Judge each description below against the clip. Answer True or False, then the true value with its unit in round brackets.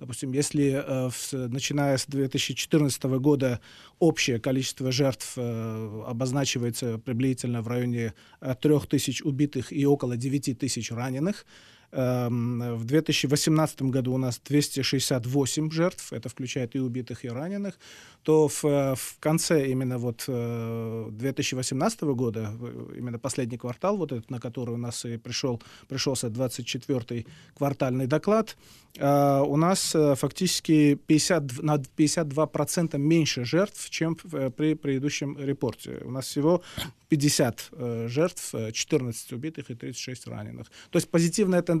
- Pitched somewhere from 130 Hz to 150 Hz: True (135 Hz)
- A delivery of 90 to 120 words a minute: True (115 wpm)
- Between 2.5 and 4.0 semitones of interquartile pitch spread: True (3.4 semitones)